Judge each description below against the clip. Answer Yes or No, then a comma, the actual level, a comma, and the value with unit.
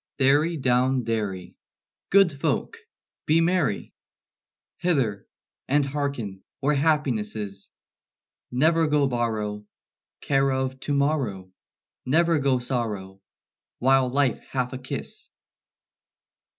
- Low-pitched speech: Yes, low, 130 Hz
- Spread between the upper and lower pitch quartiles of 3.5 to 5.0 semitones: Yes, average, 4.5 semitones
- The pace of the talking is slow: Yes, slow, 100 wpm